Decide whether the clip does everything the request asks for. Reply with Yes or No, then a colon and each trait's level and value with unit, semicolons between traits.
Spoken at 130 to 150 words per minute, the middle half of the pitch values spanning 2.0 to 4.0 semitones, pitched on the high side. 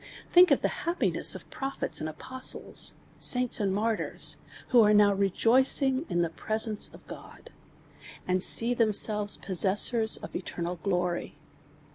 No: average, 145 wpm; average, 4.7 semitones; high, 215 Hz